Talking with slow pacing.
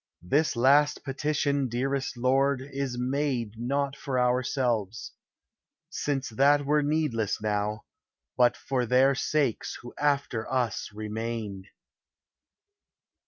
Yes: slow, 105 wpm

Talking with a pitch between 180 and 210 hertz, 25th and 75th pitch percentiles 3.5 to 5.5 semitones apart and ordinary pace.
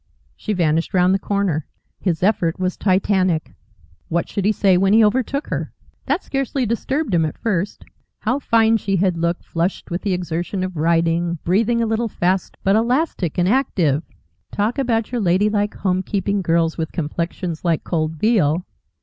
Yes: high, 190 Hz; average, 4.3 semitones; average, 165 wpm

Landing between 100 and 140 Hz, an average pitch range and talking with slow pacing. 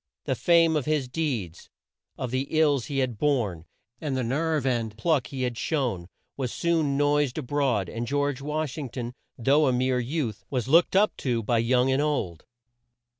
No: low, 135 Hz; average, 3.7 semitones; average, 185 wpm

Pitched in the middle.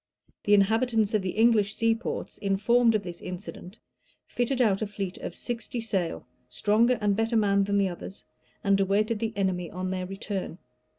No: high, 205 Hz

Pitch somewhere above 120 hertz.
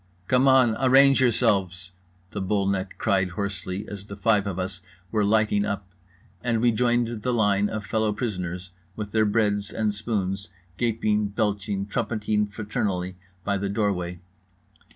No: low, 105 Hz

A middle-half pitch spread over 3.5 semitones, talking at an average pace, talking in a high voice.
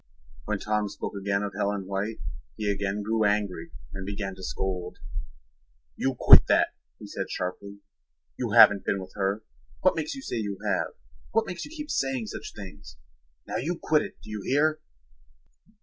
No: average, 4.3 semitones; average, 175 wpm; low, 105 Hz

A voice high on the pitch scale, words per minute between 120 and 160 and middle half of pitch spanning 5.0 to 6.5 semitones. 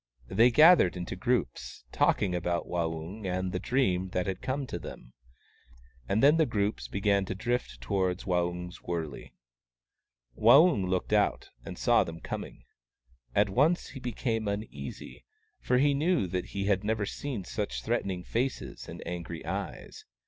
No: low, 100 Hz; average, 155 wpm; wide, 5.6 semitones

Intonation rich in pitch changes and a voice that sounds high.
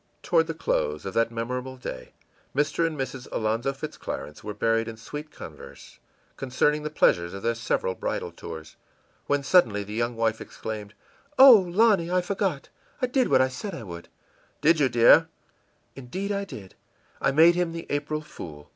No: wide, 7.0 semitones; low, 135 Hz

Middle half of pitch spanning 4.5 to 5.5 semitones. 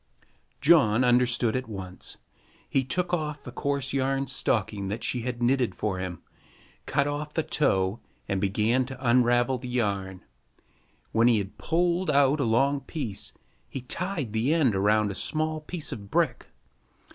Yes: average, 4.9 semitones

